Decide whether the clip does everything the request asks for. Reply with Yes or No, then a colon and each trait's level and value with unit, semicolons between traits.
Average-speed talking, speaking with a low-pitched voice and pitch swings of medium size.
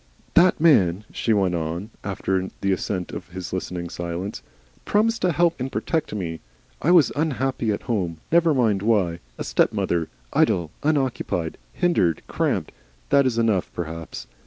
No: average, 150 wpm; low, 100 Hz; wide, 8.3 semitones